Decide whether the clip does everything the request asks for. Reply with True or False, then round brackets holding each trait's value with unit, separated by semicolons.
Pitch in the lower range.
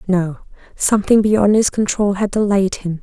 False (200 Hz)